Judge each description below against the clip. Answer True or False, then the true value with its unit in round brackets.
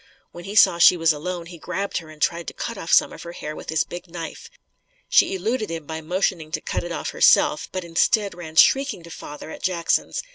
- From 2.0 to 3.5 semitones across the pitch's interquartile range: True (2.4 semitones)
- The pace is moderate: False (230 wpm)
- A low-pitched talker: False (170 Hz)